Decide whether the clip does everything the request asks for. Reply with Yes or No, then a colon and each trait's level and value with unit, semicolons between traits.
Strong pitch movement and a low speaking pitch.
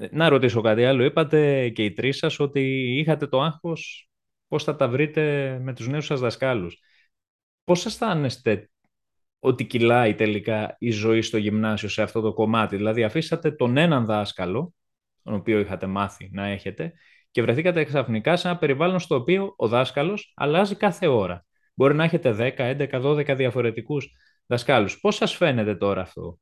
Yes: wide, 5.9 semitones; low, 130 Hz